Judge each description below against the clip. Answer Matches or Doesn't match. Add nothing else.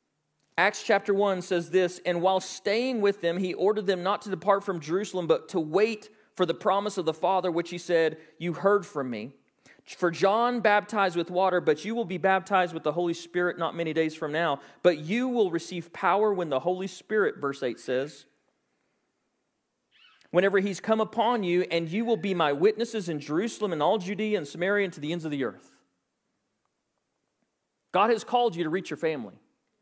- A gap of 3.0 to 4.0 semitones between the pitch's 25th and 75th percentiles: Matches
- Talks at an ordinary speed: Matches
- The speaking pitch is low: Doesn't match